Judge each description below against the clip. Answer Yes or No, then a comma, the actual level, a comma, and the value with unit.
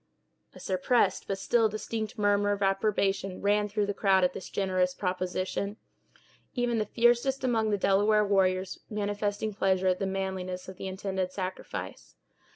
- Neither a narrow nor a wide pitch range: No, narrow, 2.0 semitones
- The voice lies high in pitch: Yes, high, 200 Hz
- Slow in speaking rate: No, average, 155 wpm